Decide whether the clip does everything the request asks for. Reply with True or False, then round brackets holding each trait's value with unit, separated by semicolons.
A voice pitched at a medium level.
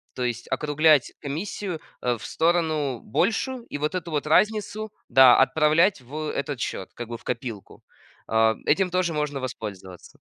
True (145 Hz)